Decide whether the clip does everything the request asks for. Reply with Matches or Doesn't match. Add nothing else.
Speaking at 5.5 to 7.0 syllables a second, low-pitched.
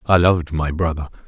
Matches